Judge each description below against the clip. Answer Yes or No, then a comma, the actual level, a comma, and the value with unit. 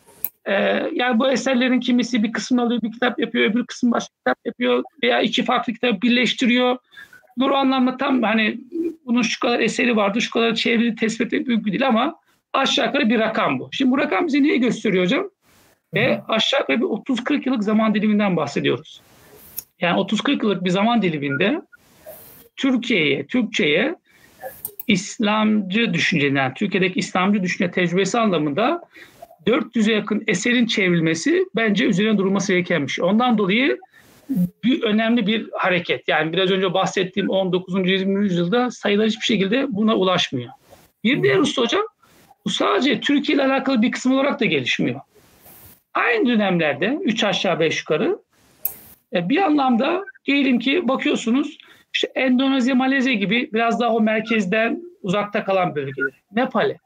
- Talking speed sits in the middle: No, fast, 145 wpm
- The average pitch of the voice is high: Yes, high, 230 Hz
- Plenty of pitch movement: No, average, 4.3 semitones